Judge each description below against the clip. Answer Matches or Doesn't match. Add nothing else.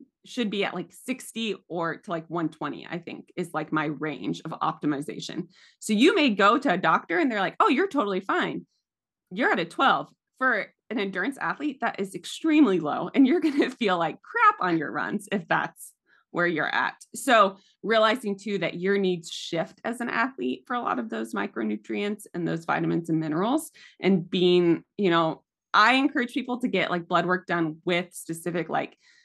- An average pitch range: Doesn't match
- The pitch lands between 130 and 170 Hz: Doesn't match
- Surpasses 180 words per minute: Matches